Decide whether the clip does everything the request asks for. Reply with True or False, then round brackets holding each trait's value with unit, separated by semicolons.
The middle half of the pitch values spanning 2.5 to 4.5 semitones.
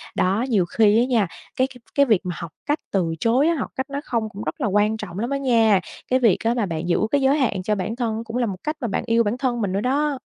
True (4.2 semitones)